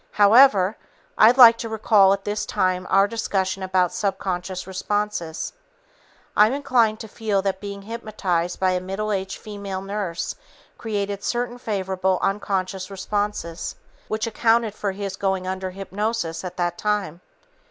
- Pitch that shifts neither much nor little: No, narrow, 2.3 semitones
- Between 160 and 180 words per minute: No, average, 140 wpm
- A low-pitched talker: No, high, 200 Hz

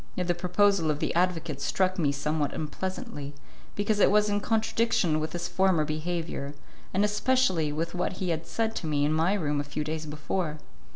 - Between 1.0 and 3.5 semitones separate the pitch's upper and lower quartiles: No, average, 4.1 semitones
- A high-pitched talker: No, medium, 170 Hz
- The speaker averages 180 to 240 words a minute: Yes, average, 190 wpm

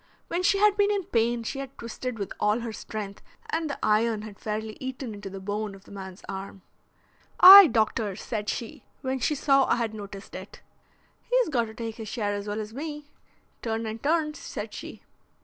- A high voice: Yes, high, 225 Hz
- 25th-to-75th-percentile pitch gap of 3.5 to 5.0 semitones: Yes, average, 4.7 semitones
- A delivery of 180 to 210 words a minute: Yes, average, 200 wpm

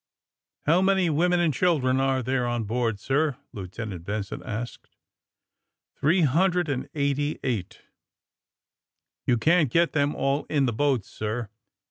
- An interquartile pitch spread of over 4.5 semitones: Yes, average, 5.0 semitones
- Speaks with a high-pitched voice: No, low, 135 Hz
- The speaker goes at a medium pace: Yes, average, 165 wpm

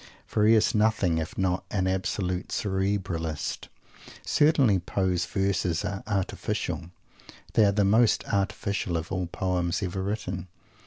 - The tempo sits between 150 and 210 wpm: No, slow, 135 wpm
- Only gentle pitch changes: Yes, narrow, 2.3 semitones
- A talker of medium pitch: No, very low, 95 Hz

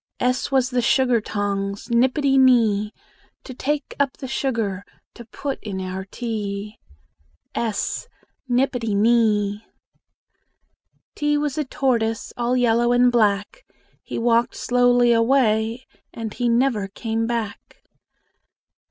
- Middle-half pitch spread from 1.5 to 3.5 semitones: Yes, average, 3.1 semitones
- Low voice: No, high, 235 Hz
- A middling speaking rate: No, slow, 115 wpm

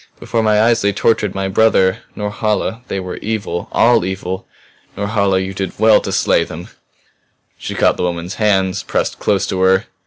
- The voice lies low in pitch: Yes, low, 100 Hz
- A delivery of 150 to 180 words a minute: Yes, average, 175 wpm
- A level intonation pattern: Yes, narrow, 2.3 semitones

